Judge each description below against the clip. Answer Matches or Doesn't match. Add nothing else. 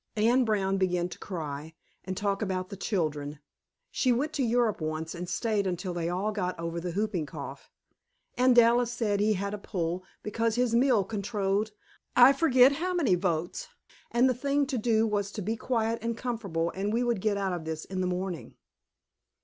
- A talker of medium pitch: Doesn't match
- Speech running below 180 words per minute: Doesn't match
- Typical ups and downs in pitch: Matches